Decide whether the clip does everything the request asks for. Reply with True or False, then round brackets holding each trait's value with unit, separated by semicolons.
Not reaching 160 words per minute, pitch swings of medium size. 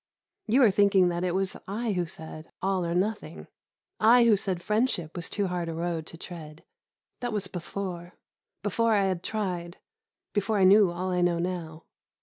False (180 wpm; 3.1 semitones)